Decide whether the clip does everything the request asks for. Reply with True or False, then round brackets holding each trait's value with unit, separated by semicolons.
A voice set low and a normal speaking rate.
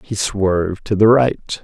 True (105 Hz; 185 wpm)